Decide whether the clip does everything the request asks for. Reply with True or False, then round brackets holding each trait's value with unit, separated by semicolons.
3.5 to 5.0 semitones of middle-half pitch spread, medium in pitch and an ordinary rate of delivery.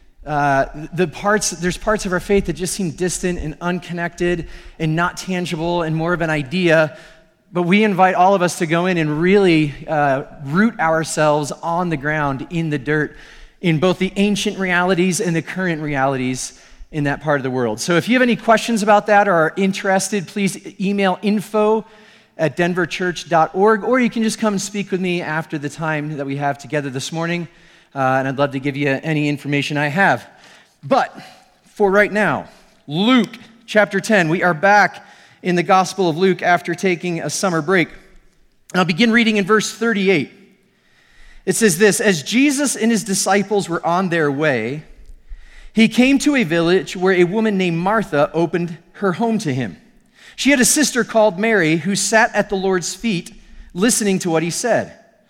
True (4.4 semitones; 180 Hz; 190 wpm)